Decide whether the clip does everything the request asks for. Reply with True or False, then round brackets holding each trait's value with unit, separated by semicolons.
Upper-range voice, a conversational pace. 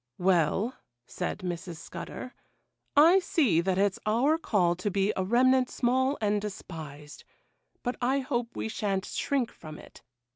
True (210 Hz; 145 wpm)